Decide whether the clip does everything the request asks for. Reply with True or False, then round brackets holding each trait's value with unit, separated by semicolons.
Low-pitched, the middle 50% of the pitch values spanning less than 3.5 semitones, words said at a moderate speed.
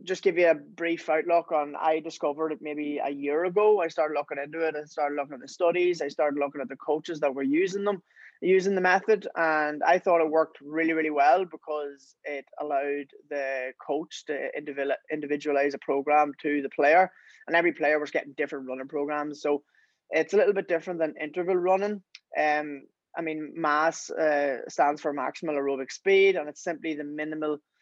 False (155 Hz; 2.7 semitones; 195 wpm)